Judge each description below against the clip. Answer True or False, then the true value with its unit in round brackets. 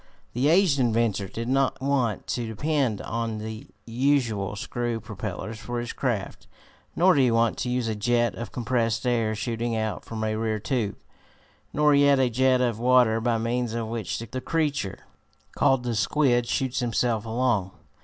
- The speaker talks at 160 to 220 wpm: True (170 wpm)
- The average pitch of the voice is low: True (120 Hz)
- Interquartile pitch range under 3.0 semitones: True (2.6 semitones)